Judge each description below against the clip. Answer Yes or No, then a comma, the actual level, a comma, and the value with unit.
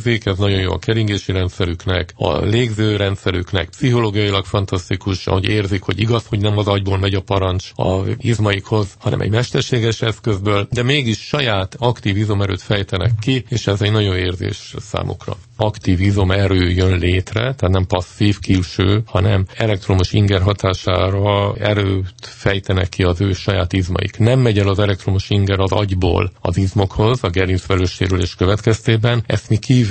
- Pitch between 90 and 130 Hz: Yes, low, 100 Hz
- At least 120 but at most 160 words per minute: Yes, fast, 155 wpm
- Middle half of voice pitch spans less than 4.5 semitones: Yes, narrow, 2.5 semitones